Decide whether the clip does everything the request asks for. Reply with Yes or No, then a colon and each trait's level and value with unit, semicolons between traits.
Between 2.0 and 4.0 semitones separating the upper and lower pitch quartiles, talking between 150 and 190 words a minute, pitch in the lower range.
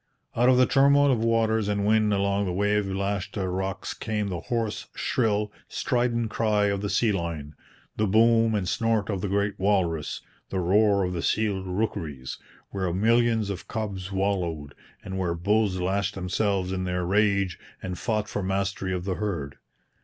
Yes: average, 2.8 semitones; average, 170 wpm; low, 100 Hz